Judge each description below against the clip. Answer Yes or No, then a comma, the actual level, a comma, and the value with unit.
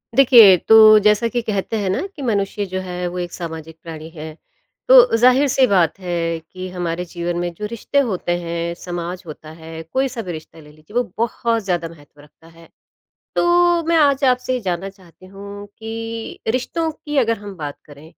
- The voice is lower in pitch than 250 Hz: Yes, high, 190 Hz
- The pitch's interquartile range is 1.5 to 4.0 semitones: No, wide, 5.6 semitones